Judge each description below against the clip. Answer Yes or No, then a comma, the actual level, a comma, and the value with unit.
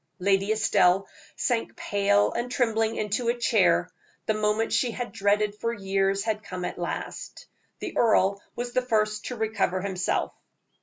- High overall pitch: Yes, high, 210 Hz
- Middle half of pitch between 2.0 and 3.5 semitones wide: Yes, narrow, 2.5 semitones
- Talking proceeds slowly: No, average, 155 wpm